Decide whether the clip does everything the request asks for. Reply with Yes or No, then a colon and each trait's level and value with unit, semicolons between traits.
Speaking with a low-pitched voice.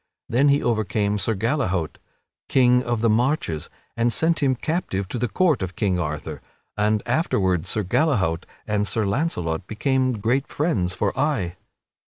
Yes: low, 110 Hz